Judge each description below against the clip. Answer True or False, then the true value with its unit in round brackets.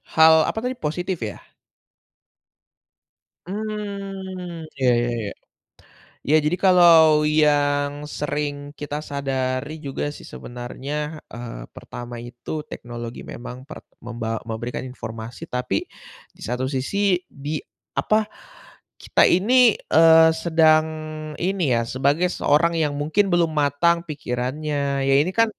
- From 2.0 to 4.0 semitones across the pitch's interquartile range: False (5.3 semitones)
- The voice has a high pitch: False (150 Hz)